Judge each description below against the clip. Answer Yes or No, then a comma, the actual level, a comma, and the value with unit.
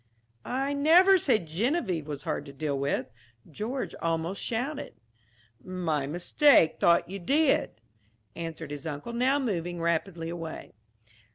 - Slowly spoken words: Yes, slow, 125 wpm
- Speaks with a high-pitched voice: No, medium, 175 Hz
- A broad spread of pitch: Yes, wide, 8.2 semitones